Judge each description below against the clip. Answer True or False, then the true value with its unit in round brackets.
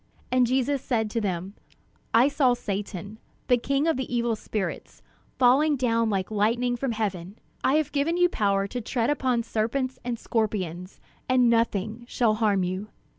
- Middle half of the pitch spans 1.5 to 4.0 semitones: True (3.6 semitones)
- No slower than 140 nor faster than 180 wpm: True (165 wpm)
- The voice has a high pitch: True (230 Hz)